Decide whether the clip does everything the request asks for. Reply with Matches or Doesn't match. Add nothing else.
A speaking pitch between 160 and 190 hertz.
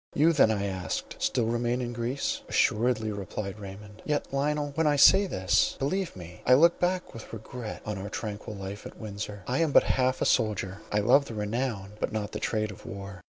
Doesn't match